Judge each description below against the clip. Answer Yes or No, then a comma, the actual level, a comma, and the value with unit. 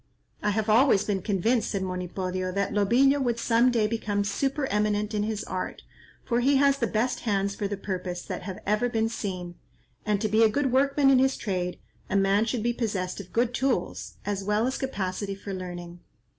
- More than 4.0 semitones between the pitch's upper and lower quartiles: No, average, 3.7 semitones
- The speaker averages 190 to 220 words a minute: Yes, average, 200 wpm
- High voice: Yes, high, 210 Hz